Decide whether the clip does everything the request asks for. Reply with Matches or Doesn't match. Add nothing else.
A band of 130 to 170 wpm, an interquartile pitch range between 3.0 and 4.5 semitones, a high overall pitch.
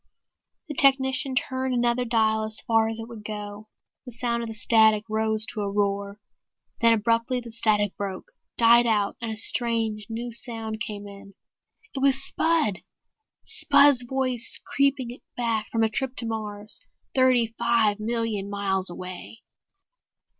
Doesn't match